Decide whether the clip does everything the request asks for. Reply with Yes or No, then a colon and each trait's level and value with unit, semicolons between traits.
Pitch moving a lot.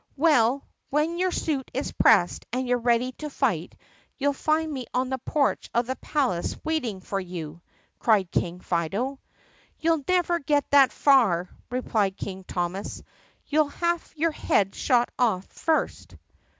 Yes: wide, 7.3 semitones